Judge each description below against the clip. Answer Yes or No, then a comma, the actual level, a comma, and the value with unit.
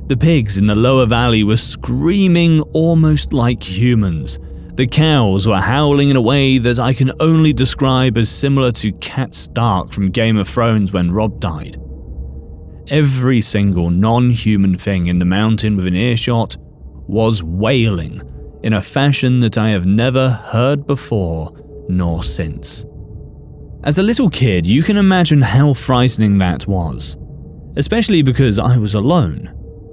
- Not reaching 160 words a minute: Yes, average, 150 wpm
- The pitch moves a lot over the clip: Yes, wide, 5.7 semitones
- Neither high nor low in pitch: No, low, 115 Hz